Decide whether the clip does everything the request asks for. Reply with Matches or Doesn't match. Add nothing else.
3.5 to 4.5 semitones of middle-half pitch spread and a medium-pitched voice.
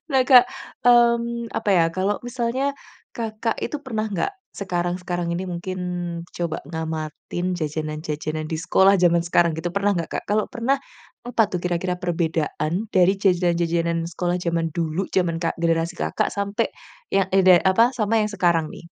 Matches